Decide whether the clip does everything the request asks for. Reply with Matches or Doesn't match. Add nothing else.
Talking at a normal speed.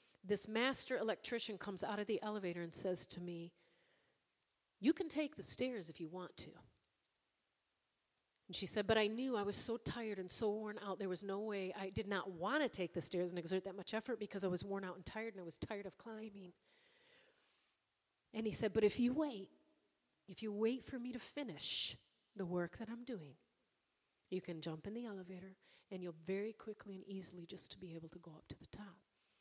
Doesn't match